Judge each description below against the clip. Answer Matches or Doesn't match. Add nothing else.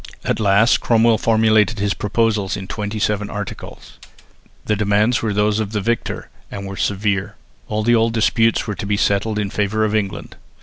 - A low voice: Matches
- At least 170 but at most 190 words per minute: Matches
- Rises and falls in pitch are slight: Matches